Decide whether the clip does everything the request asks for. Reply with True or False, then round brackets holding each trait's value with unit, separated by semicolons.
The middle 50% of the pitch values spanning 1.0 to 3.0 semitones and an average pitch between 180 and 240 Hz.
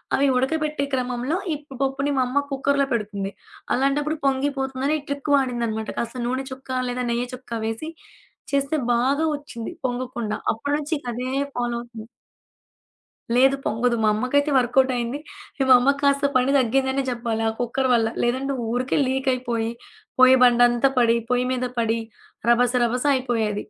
False (2.4 semitones; 255 Hz)